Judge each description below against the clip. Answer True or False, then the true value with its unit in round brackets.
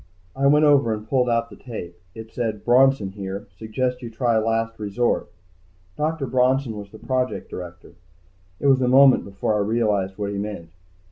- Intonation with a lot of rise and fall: False (3.8 semitones)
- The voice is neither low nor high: False (115 Hz)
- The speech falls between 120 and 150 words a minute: False (180 wpm)